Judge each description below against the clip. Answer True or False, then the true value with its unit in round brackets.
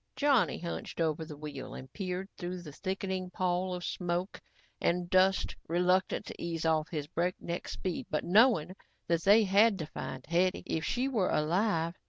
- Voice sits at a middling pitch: True (180 Hz)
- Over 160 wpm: True (170 wpm)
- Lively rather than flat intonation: False (2.6 semitones)